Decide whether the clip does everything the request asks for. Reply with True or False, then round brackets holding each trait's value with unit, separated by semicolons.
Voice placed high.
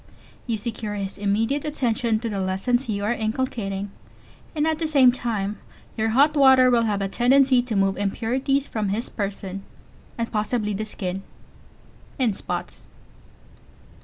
True (225 Hz)